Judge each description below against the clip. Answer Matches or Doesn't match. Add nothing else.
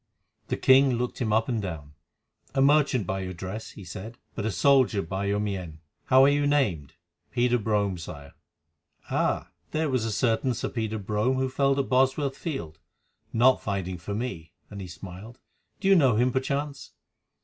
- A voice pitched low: Matches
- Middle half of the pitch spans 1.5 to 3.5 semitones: Doesn't match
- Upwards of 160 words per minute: Matches